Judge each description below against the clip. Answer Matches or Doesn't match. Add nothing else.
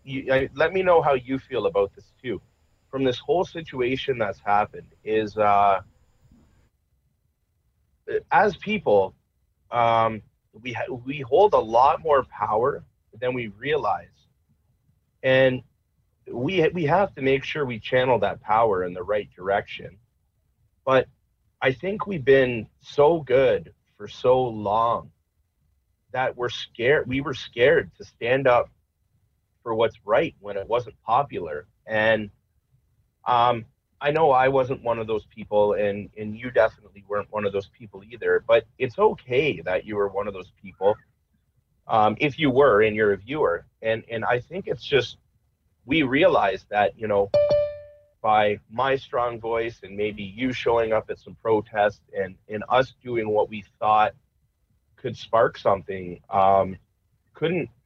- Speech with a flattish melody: Doesn't match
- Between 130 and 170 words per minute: Matches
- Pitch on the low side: Matches